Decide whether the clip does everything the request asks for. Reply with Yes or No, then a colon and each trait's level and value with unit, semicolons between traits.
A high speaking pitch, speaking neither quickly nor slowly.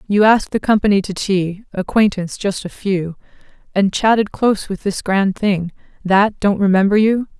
Yes: high, 200 Hz; average, 170 wpm